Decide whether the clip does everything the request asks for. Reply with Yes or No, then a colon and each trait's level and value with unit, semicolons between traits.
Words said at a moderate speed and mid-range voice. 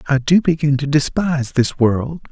Yes: average, 180 wpm; medium, 145 Hz